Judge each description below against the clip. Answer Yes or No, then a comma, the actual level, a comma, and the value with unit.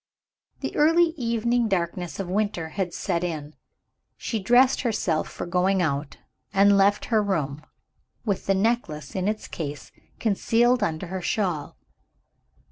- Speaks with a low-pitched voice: No, high, 195 Hz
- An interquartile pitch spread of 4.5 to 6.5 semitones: Yes, average, 4.8 semitones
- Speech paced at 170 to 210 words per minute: No, slow, 135 wpm